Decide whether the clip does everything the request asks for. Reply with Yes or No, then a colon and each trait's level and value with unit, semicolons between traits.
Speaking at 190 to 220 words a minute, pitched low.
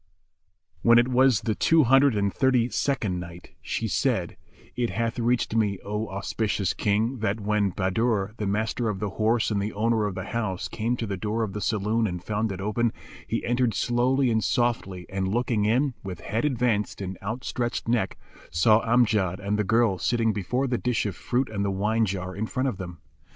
Yes: average, 200 wpm; low, 110 Hz